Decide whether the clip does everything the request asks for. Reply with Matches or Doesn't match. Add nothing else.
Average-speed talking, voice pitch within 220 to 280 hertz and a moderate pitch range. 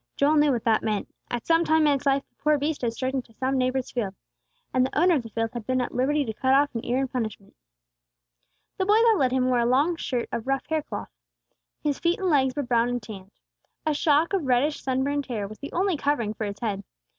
Doesn't match